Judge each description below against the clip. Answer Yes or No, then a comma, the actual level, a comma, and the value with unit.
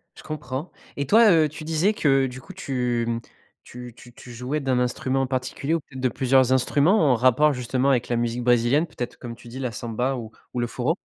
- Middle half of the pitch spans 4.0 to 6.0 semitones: No, average, 2.8 semitones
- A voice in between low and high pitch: No, low, 130 Hz